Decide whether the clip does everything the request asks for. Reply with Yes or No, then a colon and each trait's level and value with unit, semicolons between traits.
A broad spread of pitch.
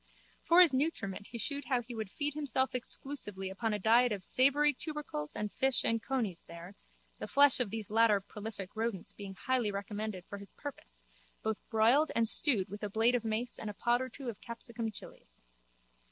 No: average, 4.1 semitones